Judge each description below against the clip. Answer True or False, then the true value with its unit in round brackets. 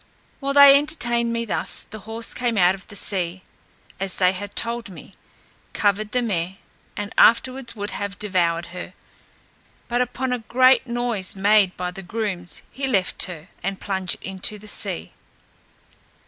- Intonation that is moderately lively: True (4.1 semitones)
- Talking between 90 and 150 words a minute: False (160 wpm)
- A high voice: True (205 Hz)